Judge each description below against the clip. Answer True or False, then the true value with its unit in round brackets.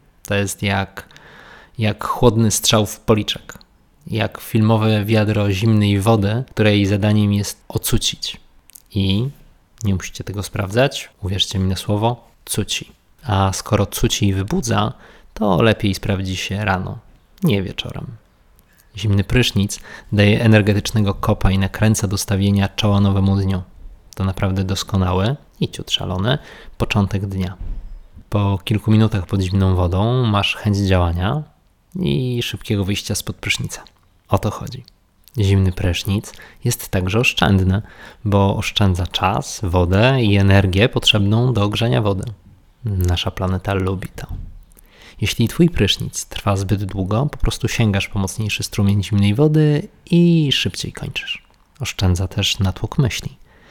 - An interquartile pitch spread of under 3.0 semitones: True (2.5 semitones)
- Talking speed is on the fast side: False (130 wpm)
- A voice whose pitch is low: True (100 Hz)